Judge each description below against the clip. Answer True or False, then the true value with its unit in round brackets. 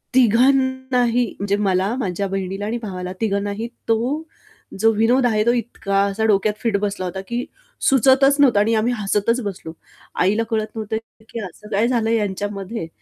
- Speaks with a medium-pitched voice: False (215 Hz)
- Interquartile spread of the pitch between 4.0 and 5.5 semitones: False (3.1 semitones)